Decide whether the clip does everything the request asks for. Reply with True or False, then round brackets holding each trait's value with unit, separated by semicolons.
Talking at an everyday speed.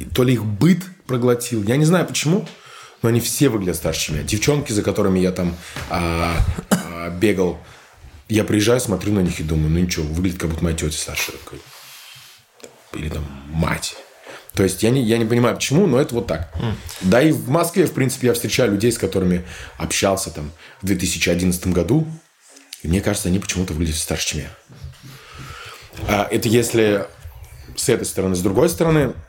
False (175 wpm)